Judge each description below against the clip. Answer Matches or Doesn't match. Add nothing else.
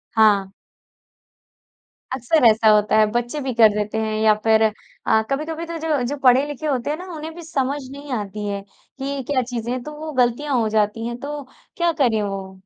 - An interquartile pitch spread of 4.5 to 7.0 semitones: Matches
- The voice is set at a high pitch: Matches